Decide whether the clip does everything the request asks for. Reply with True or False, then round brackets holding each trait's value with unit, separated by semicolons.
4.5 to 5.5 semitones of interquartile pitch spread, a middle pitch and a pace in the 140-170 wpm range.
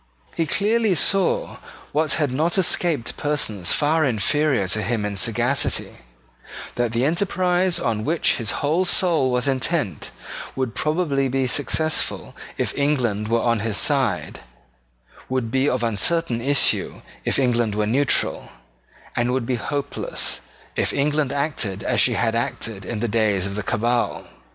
False (5.1 semitones; 130 Hz; 145 wpm)